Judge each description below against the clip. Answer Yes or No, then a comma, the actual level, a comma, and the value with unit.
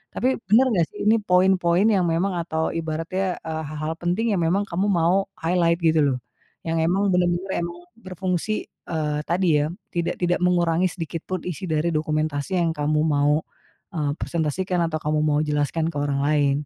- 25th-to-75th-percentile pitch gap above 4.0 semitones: No, average, 3.0 semitones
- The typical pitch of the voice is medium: Yes, medium, 170 Hz